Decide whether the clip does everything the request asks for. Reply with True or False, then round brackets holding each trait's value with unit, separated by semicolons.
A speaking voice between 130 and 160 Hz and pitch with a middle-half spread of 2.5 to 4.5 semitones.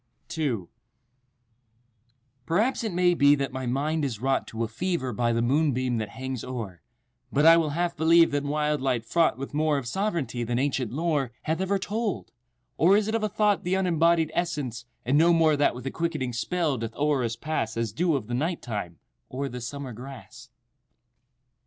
False (140 Hz; 5.3 semitones)